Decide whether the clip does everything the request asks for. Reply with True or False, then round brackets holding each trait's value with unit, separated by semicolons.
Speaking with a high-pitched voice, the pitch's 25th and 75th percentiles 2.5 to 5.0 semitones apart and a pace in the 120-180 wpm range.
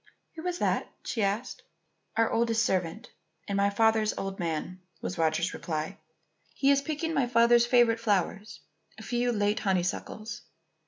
True (220 Hz; 3.9 semitones; 150 wpm)